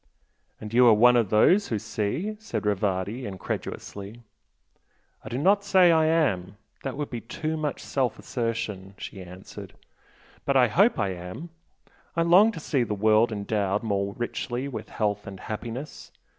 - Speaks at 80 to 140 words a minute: No, average, 165 wpm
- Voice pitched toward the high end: No, low, 115 Hz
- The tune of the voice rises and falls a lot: Yes, wide, 6.5 semitones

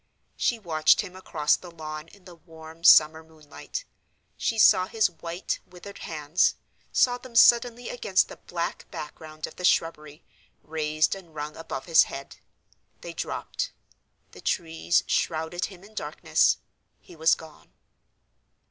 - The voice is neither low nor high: Yes, medium, 165 Hz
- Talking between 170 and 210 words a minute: No, slow, 135 wpm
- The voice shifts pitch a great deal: No, average, 3.2 semitones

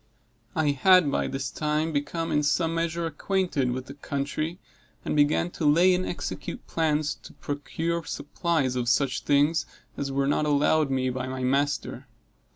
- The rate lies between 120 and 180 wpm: Yes, average, 160 wpm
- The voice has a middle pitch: Yes, medium, 145 Hz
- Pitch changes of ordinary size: Yes, average, 3.0 semitones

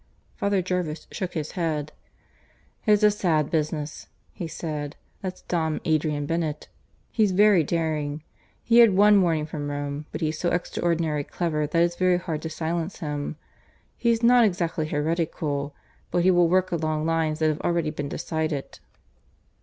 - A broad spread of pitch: No, average, 2.9 semitones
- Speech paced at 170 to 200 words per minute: No, average, 155 wpm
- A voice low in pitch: No, medium, 160 Hz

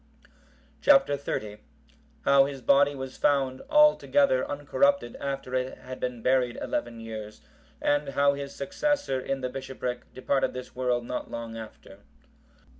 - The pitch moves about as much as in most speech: No, narrow, 2.3 semitones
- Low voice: Yes, low, 130 Hz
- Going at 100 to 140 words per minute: Yes, slow, 135 wpm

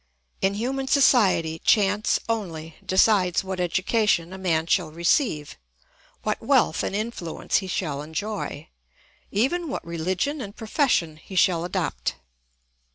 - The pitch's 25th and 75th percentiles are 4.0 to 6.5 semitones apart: Yes, average, 4.9 semitones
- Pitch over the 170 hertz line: Yes, high, 190 Hz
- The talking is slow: Yes, slow, 125 wpm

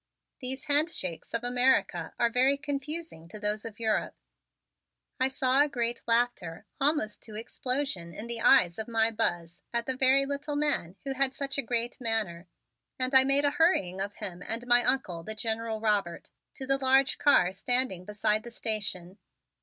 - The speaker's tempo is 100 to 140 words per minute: No, average, 175 wpm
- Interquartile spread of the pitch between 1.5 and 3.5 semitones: No, average, 4.4 semitones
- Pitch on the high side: Yes, high, 235 Hz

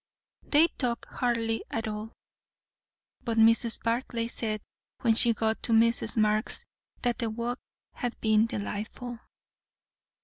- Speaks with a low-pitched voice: No, high, 230 Hz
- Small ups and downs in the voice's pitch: Yes, narrow, 1.4 semitones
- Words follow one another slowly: Yes, slow, 125 wpm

